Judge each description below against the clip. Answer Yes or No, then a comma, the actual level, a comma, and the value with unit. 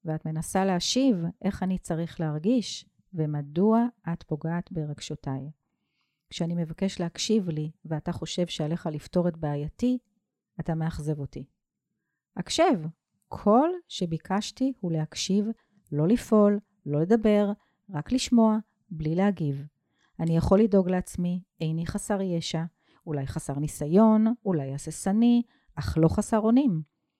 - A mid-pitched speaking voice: Yes, medium, 175 Hz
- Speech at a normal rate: Yes, average, 115 wpm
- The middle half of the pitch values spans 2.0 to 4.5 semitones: No, average, 5.0 semitones